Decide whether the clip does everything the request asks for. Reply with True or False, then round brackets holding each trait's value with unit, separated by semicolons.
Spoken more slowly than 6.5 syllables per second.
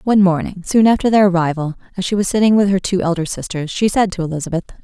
False (6.9 syllables/s)